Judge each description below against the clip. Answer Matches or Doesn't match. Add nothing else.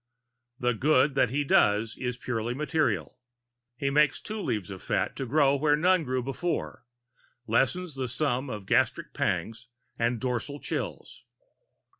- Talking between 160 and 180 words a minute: Doesn't match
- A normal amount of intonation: Matches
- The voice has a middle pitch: Doesn't match